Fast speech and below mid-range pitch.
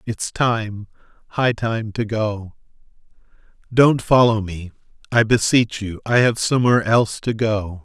No: average, 140 wpm; low, 110 Hz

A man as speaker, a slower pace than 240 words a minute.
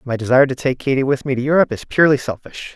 No: male; fast, 260 wpm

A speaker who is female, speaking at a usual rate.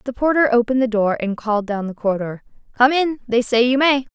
No: female; fast, 230 wpm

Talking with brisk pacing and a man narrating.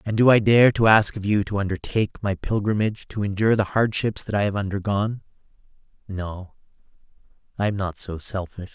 No: average, 180 wpm; male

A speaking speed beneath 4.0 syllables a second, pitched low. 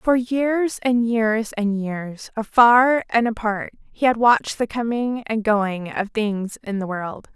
No: 3.7 syllables/s; high, 225 Hz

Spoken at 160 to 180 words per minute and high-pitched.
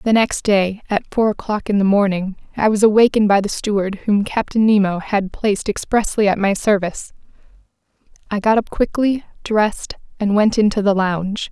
Yes: average, 175 wpm; high, 205 Hz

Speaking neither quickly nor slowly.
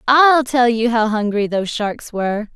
Yes: average, 190 wpm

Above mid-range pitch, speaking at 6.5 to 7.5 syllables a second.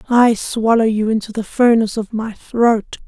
No: high, 225 Hz; 4.6 syllables/s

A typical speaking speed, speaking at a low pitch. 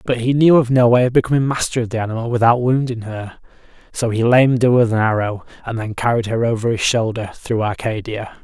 No: fast, 220 wpm; low, 115 Hz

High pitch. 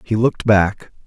No: low, 105 Hz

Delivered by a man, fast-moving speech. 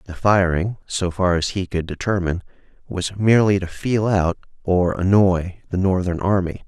No: male; average, 160 wpm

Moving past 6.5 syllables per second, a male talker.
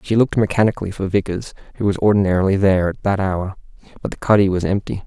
Yes: 7.0 syllables/s; male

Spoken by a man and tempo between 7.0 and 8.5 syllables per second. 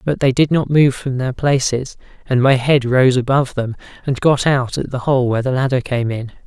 No: male; 5.3 syllables/s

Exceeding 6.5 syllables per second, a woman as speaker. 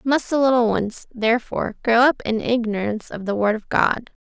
No: 5.4 syllables/s; female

